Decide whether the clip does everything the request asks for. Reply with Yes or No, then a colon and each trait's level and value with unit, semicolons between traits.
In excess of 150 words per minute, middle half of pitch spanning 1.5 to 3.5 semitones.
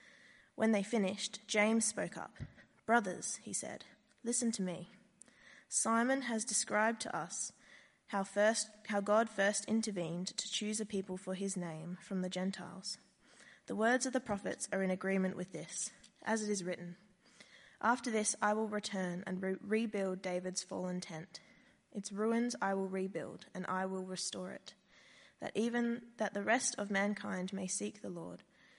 Yes: average, 165 wpm; average, 2.8 semitones